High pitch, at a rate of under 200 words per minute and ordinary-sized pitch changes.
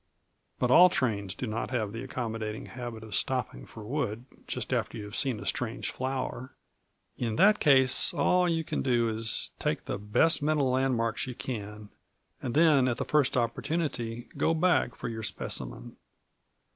No: low, 125 Hz; average, 170 wpm; average, 3.8 semitones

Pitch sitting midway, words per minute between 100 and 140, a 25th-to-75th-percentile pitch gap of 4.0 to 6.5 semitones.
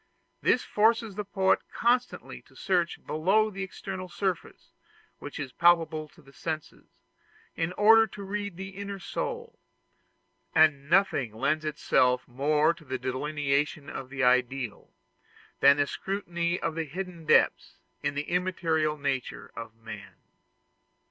Yes: medium, 165 Hz; slow, 135 wpm; wide, 5.4 semitones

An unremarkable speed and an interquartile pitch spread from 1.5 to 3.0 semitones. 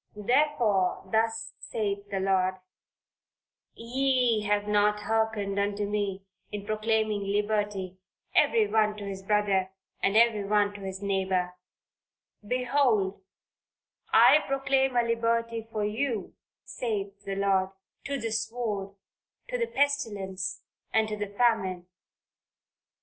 No: slow, 115 wpm; average, 2.7 semitones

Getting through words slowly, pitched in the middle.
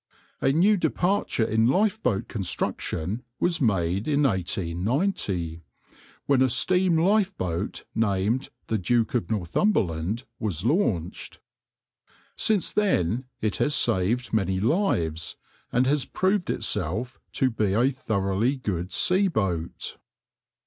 No: slow, 115 wpm; low, 115 Hz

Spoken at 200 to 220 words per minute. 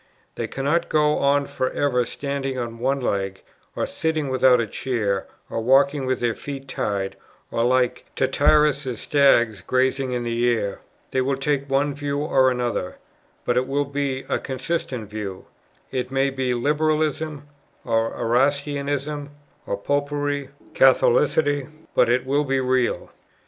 No: average, 150 wpm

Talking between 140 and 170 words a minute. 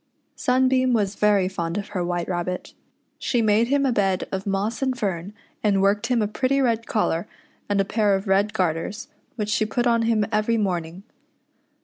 No: average, 190 wpm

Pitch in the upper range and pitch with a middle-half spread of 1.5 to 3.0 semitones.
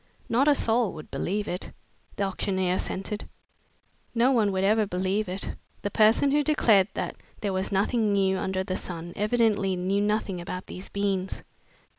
Yes: high, 200 Hz; narrow, 2.4 semitones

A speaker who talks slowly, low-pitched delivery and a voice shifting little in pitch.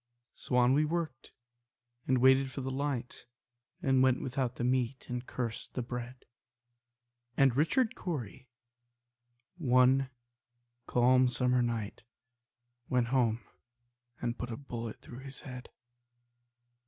Yes: slow, 120 wpm; low, 125 Hz; narrow, 1.6 semitones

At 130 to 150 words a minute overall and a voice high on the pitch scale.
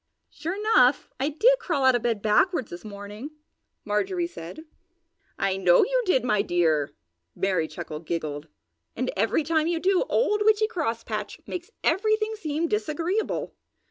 Yes: average, 145 wpm; very high, 280 Hz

